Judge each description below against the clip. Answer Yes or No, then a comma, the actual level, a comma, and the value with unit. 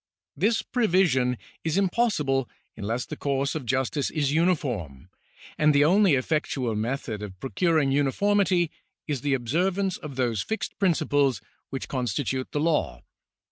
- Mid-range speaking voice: Yes, medium, 145 Hz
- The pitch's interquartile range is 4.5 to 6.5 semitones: Yes, average, 5.2 semitones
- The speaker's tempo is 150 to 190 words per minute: No, slow, 135 wpm